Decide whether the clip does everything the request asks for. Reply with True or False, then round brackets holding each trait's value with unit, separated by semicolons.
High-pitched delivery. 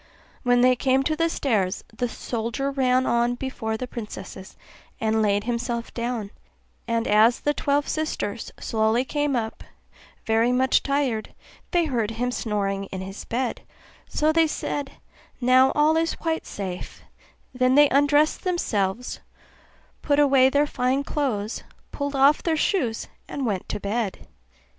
True (250 Hz)